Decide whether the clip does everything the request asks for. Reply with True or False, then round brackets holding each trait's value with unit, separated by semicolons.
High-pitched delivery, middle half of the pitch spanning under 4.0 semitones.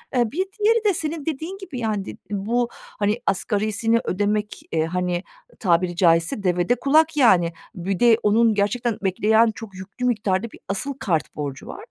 False (210 Hz; 4.7 semitones)